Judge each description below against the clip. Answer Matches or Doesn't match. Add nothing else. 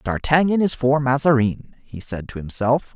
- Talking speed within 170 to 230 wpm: Doesn't match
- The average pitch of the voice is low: Matches